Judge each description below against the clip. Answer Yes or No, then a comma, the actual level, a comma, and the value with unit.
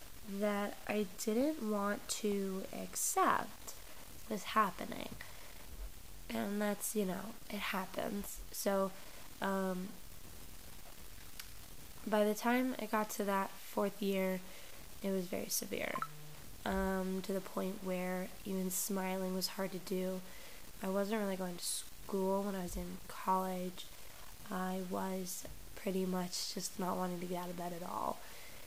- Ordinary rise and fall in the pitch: No, narrow, 2.0 semitones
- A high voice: Yes, high, 195 Hz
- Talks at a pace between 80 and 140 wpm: Yes, slow, 135 wpm